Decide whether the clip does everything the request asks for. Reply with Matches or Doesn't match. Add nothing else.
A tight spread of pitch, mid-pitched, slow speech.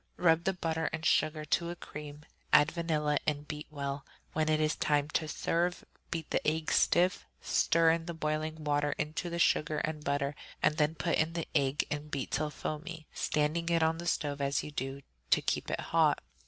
Doesn't match